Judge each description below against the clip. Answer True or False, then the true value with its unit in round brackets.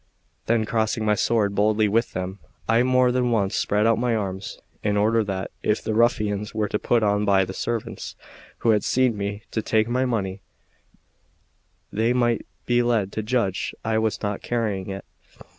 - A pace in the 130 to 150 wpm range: False (175 wpm)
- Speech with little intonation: True (2.3 semitones)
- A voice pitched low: True (110 Hz)